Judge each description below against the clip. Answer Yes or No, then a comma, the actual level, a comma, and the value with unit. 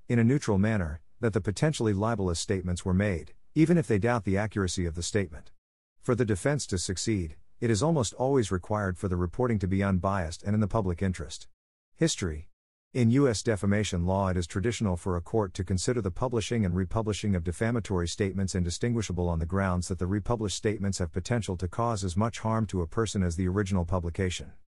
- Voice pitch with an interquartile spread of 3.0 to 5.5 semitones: Yes, average, 3.9 semitones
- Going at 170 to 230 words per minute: Yes, average, 200 wpm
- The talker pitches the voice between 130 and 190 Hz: No, low, 100 Hz